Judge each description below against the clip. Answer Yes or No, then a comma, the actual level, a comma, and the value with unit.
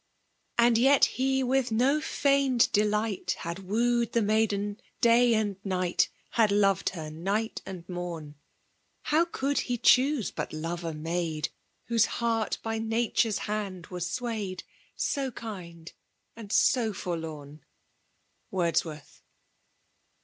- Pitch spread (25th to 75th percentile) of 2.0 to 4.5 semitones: No, average, 5.0 semitones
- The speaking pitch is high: Yes, high, 210 Hz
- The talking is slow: Yes, slow, 125 wpm